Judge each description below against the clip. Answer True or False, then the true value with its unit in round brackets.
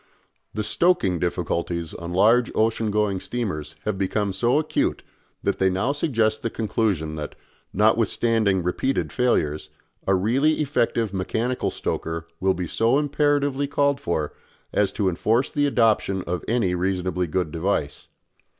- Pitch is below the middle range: True (105 Hz)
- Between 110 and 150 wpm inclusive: True (140 wpm)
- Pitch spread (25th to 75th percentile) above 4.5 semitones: True (5.3 semitones)